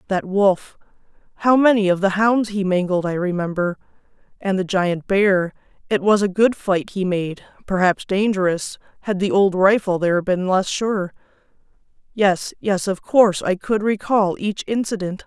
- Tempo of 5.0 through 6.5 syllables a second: No, 4.5 syllables/s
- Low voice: No, high, 195 Hz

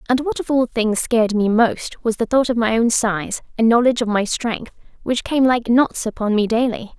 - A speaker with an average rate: No, fast, 230 wpm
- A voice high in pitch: Yes, high, 230 Hz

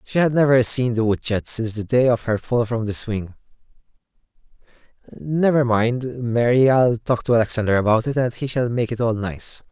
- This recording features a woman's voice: No, male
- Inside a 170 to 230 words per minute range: Yes, average, 200 wpm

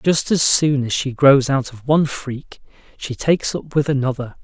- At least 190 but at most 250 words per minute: Yes, fast, 205 wpm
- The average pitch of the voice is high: No, medium, 140 Hz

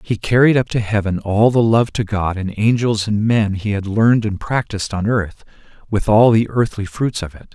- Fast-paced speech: Yes, fast, 225 wpm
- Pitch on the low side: Yes, low, 105 Hz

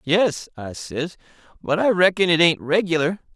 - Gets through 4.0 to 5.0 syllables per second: Yes, 4.5 syllables/s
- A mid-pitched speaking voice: Yes, medium, 170 Hz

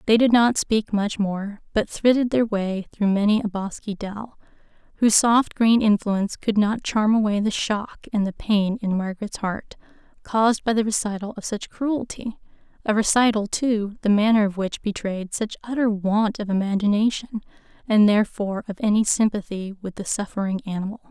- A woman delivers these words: Yes, female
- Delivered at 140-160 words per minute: No, average, 170 wpm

